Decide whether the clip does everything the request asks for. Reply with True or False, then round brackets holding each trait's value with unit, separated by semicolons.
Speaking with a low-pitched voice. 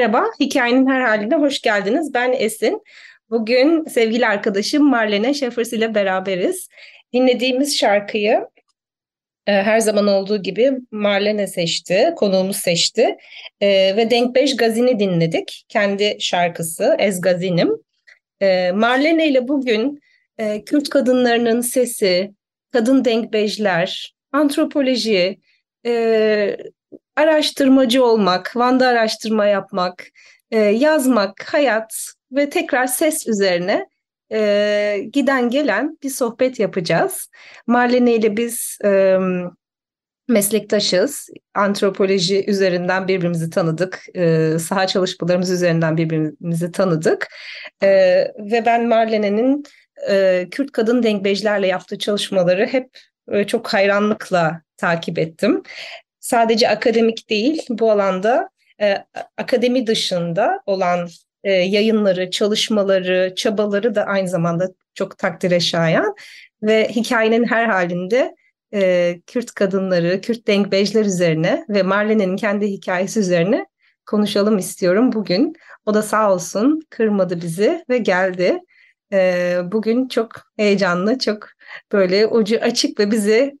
False (215 Hz)